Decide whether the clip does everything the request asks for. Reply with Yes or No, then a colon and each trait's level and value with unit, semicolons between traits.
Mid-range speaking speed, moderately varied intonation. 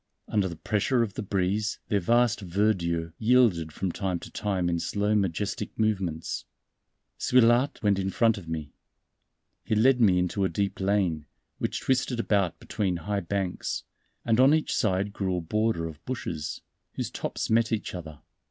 Yes: average, 165 wpm; average, 3.8 semitones